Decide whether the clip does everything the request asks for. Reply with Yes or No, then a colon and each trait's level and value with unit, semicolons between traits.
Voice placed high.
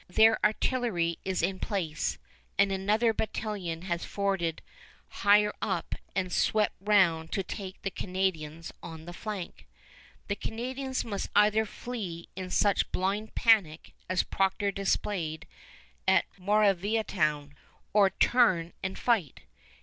Yes: high, 195 Hz